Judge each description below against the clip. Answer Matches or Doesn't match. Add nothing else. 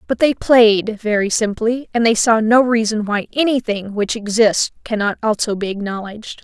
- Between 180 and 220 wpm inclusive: Doesn't match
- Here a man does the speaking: Doesn't match